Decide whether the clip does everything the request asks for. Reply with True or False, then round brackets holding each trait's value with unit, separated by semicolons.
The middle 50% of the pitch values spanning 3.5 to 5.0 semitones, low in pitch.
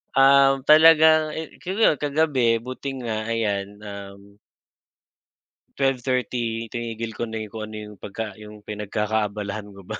True (4.4 semitones; 115 Hz)